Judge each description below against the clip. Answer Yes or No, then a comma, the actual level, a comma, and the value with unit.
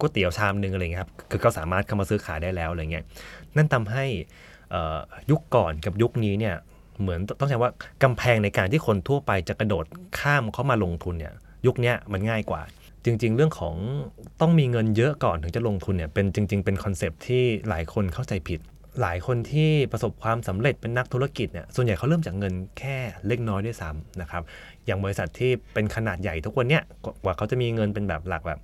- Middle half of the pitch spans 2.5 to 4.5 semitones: No, average, 5.0 semitones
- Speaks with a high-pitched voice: No, low, 105 Hz